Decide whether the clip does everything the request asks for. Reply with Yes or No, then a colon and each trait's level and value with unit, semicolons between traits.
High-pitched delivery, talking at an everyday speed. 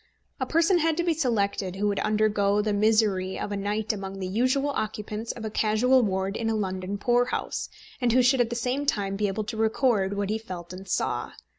No: high, 215 Hz; fast, 225 wpm